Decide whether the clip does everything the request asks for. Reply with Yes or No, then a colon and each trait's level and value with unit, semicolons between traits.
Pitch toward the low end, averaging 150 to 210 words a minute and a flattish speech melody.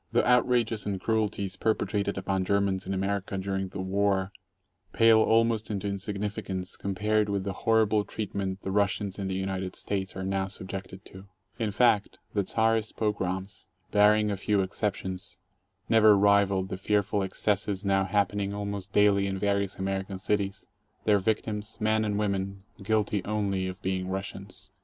Yes: low, 100 Hz; average, 155 wpm; narrow, 1.6 semitones